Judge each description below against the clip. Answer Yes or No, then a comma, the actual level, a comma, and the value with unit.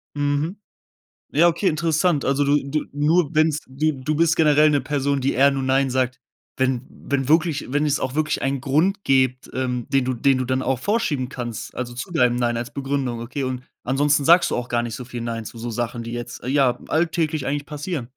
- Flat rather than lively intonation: No, average, 3.1 semitones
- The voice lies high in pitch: No, low, 135 Hz